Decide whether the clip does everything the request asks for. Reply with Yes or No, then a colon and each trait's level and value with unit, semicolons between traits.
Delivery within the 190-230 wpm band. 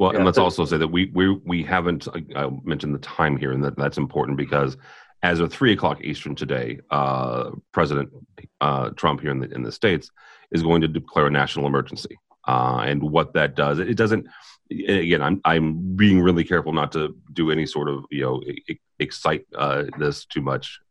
Yes: average, 200 wpm